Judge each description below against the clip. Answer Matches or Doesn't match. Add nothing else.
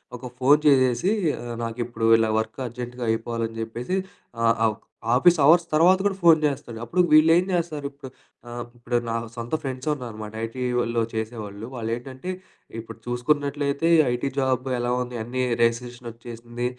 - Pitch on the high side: Doesn't match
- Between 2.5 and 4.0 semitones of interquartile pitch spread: Matches